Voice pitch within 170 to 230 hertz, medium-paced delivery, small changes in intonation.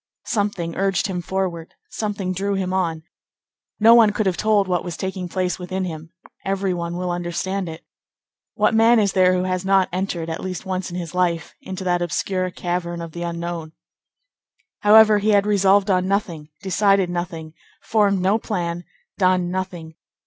Yes: medium, 185 Hz; average, 170 wpm; narrow, 2.2 semitones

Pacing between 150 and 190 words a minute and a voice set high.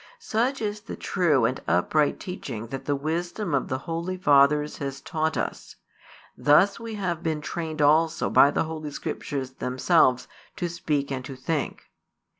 No: average, 160 wpm; medium, 155 Hz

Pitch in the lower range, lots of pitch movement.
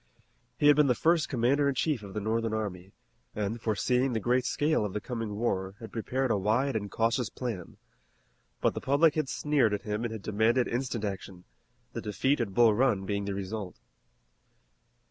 No: low, 115 Hz; average, 4.1 semitones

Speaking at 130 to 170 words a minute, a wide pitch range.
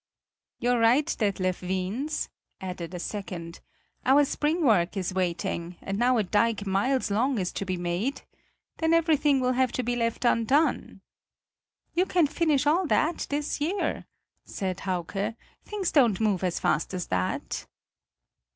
Yes: average, 150 wpm; wide, 7.3 semitones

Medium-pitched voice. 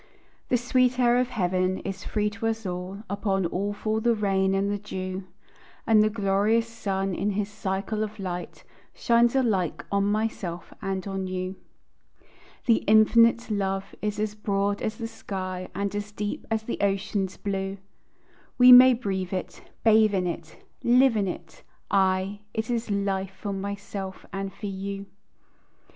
No: high, 200 Hz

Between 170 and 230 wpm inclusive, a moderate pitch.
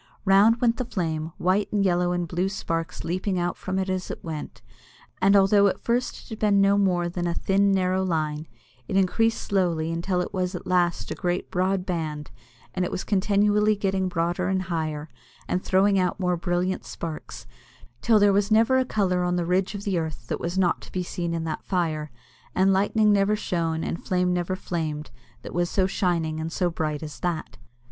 Yes: fast, 205 wpm; medium, 180 Hz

